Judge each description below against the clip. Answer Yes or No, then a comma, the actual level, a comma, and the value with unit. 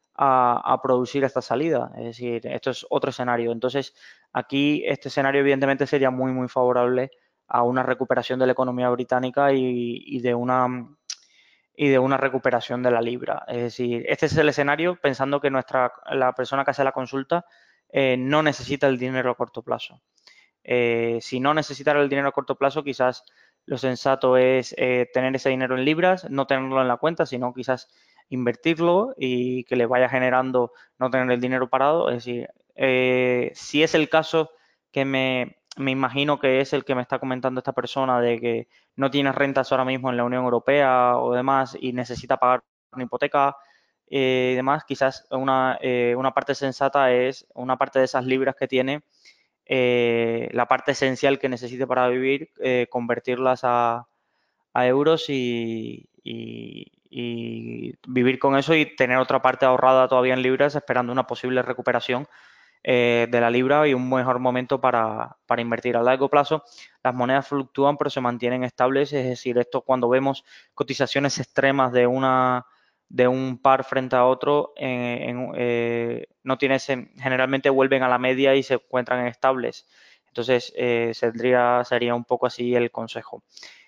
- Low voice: Yes, low, 130 Hz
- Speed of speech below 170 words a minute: No, average, 175 wpm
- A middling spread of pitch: No, narrow, 1.6 semitones